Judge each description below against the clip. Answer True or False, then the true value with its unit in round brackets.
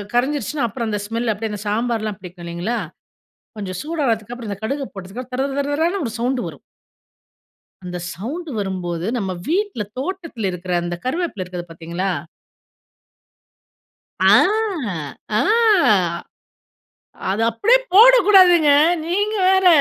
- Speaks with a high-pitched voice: True (235 Hz)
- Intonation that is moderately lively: False (8.8 semitones)